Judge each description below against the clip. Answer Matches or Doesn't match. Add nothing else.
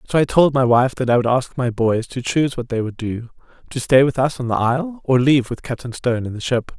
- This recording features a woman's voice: Doesn't match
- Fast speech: Matches